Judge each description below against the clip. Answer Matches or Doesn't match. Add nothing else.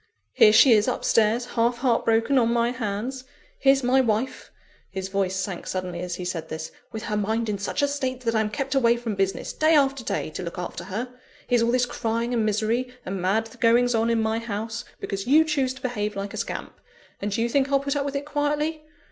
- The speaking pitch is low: Doesn't match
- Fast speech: Matches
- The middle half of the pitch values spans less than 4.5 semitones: Matches